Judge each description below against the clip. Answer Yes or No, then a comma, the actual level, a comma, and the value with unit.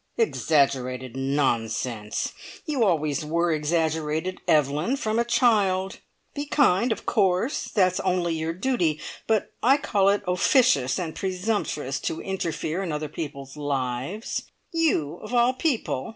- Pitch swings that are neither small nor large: No, wide, 6.6 semitones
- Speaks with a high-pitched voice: No, medium, 170 Hz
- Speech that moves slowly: Yes, slow, 130 wpm